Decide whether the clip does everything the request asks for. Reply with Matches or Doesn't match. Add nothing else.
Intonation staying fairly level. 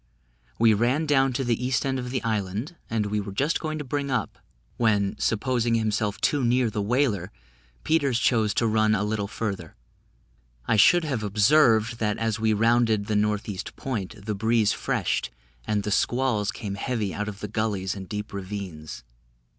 Doesn't match